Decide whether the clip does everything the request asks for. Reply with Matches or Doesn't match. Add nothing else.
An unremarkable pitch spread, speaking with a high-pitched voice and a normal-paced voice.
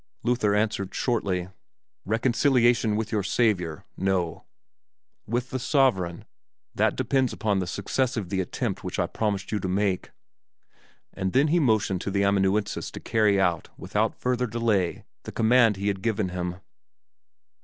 Doesn't match